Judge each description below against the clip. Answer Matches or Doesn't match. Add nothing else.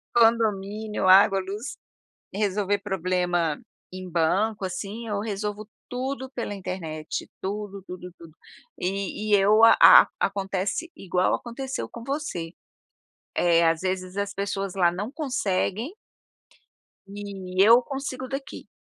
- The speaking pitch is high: Matches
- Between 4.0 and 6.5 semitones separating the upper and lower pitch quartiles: Doesn't match